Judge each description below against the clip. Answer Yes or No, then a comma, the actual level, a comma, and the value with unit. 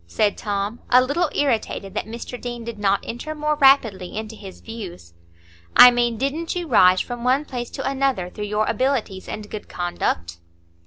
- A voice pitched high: Yes, high, 230 Hz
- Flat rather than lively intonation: No, average, 4.8 semitones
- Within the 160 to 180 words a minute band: Yes, average, 175 wpm